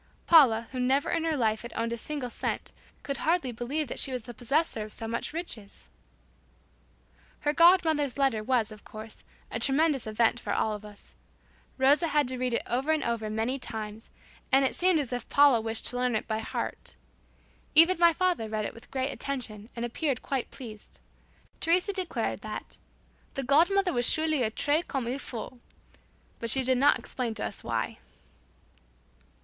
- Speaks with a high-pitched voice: Yes, very high, 255 Hz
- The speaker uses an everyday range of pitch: Yes, average, 4.8 semitones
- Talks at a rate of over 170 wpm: Yes, average, 185 wpm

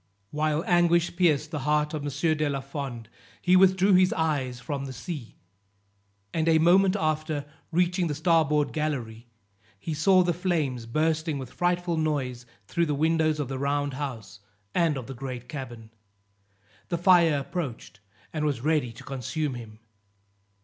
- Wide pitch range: No, average, 3.8 semitones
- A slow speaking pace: No, average, 155 wpm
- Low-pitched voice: No, medium, 150 Hz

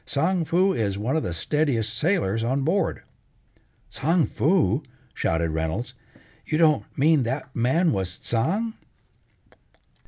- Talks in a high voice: No, low, 135 Hz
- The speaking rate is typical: No, slow, 125 wpm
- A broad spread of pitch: Yes, wide, 6.5 semitones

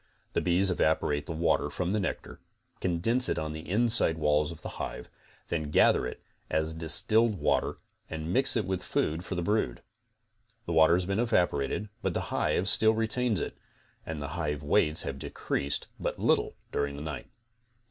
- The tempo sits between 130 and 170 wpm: No, average, 180 wpm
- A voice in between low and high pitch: No, very low, 85 Hz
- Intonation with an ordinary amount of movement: Yes, average, 4.7 semitones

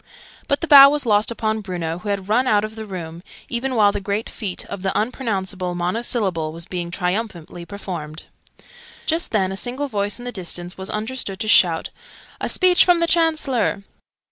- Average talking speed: Yes, average, 185 wpm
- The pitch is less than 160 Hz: No, high, 205 Hz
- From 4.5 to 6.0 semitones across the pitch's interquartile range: Yes, average, 5.0 semitones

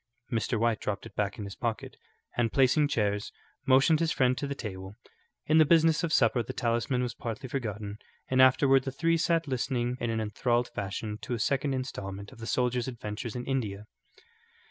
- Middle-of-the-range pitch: No, low, 125 Hz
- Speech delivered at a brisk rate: No, average, 190 wpm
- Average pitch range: Yes, average, 3.8 semitones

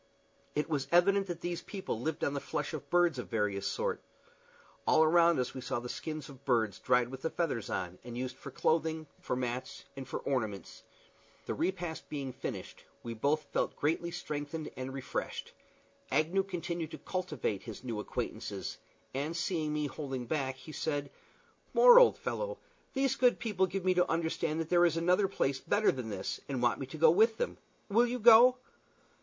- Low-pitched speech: No, medium, 155 Hz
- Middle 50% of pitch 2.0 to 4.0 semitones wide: No, wide, 5.4 semitones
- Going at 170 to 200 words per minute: Yes, average, 185 wpm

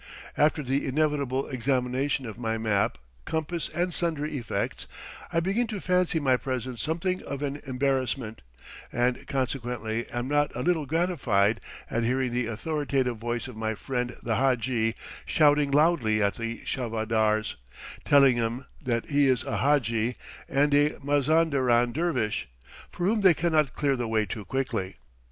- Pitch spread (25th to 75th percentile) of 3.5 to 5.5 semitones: Yes, average, 4.1 semitones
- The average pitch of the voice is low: Yes, low, 130 Hz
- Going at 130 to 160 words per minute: Yes, average, 150 wpm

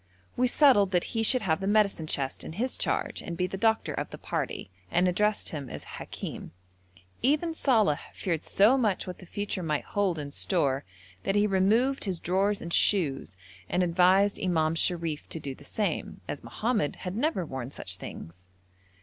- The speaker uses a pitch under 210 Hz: Yes, medium, 185 Hz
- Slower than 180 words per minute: No, average, 185 wpm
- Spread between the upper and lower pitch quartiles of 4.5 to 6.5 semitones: Yes, average, 4.8 semitones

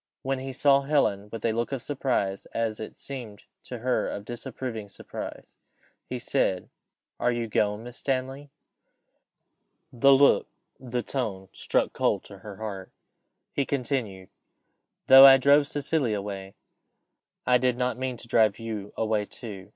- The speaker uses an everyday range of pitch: Yes, average, 4.2 semitones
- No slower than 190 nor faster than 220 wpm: No, average, 150 wpm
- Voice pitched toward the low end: Yes, low, 120 Hz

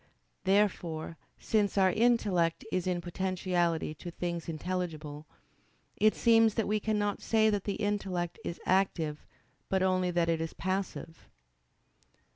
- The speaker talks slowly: Yes, slow, 130 wpm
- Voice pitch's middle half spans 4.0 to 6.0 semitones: No, average, 3.3 semitones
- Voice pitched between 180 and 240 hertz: Yes, medium, 185 Hz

